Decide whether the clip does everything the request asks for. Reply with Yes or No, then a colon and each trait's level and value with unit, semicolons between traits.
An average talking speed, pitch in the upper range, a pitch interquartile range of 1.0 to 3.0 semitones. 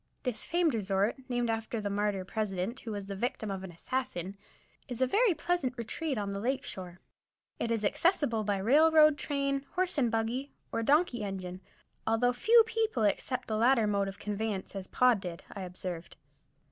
No: average, 180 wpm; high, 225 Hz; average, 5.3 semitones